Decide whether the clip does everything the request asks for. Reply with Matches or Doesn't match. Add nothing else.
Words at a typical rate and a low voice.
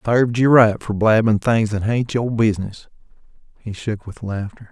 Matches